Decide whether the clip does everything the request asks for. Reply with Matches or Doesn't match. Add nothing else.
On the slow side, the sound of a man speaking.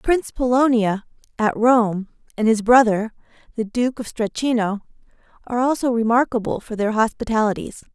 Doesn't match